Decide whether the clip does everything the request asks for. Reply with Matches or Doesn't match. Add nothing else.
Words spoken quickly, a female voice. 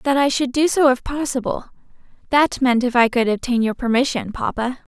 Doesn't match